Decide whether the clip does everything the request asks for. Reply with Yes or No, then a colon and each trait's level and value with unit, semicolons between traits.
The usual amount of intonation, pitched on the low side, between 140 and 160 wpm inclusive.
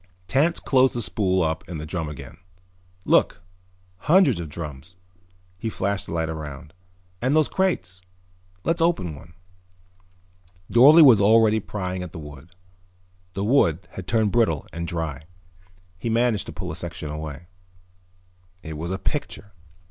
No: wide, 6.4 semitones; very low, 90 Hz; average, 150 wpm